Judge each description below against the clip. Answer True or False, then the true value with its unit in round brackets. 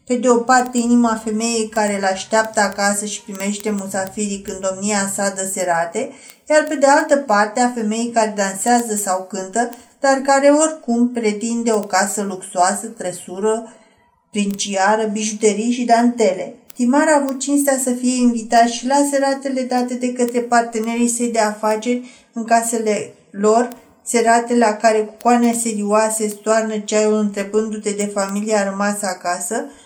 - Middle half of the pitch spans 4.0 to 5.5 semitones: False (2.7 semitones)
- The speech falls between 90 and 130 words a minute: False (150 wpm)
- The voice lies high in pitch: True (225 Hz)